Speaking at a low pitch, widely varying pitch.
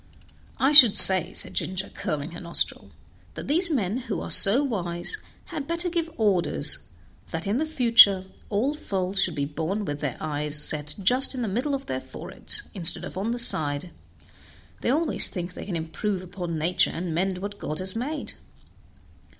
No: high, 190 Hz; wide, 6.8 semitones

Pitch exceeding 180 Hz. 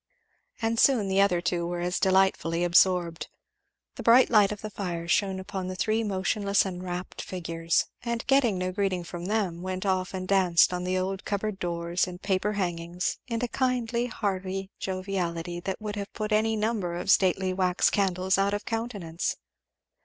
Yes: high, 190 Hz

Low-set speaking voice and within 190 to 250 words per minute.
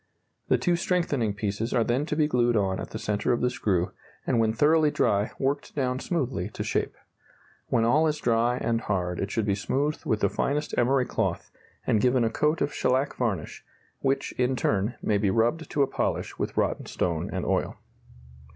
Yes: low, 120 Hz; average, 195 wpm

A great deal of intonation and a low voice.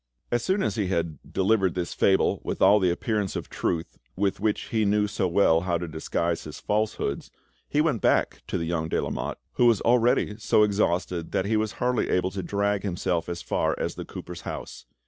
No: average, 3.7 semitones; low, 100 Hz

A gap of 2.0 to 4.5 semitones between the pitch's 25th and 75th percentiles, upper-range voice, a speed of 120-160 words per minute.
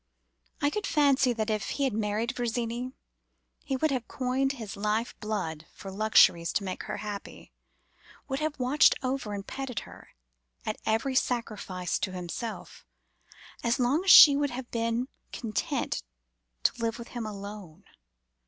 Yes: average, 4.0 semitones; high, 230 Hz; average, 155 wpm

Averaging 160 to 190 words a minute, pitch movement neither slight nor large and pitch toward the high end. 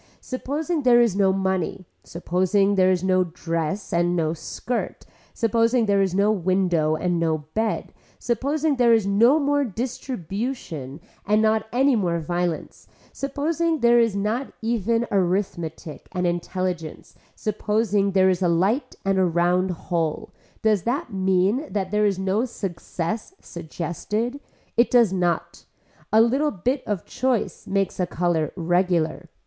No: average, 145 wpm; average, 4.9 semitones; high, 195 Hz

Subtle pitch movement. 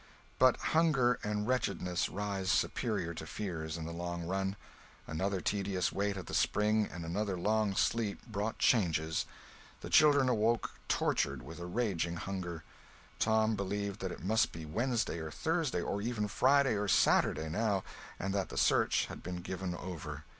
No: average, 3.9 semitones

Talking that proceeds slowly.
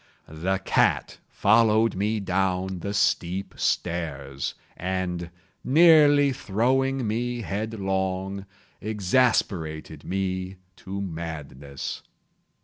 Yes: slow, 80 wpm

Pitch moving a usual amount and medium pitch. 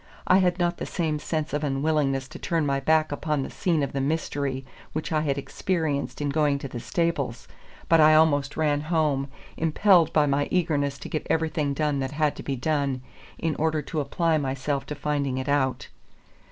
No: narrow, 2.3 semitones; medium, 150 Hz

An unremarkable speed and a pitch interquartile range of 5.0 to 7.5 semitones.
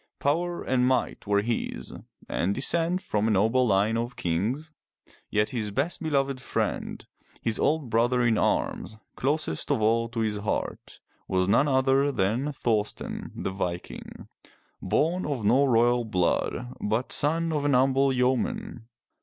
No: average, 145 wpm; average, 4.5 semitones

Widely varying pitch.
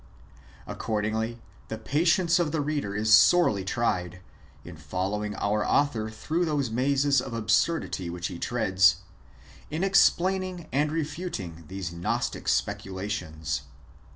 Yes: wide, 8.0 semitones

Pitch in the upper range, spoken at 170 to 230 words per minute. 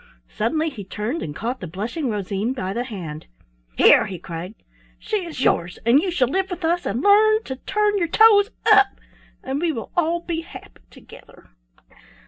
Yes: very high, 270 Hz; average, 180 wpm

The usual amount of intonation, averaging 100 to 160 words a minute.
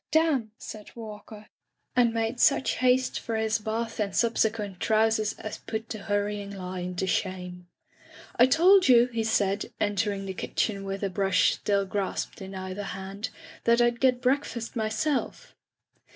Yes: average, 3.1 semitones; average, 155 wpm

